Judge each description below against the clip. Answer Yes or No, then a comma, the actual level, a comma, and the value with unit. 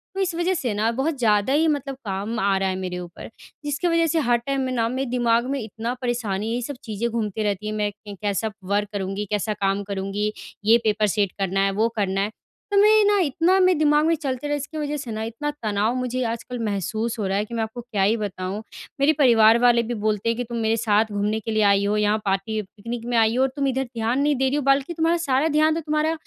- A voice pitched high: Yes, high, 230 Hz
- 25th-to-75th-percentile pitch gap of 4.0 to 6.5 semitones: Yes, average, 4.8 semitones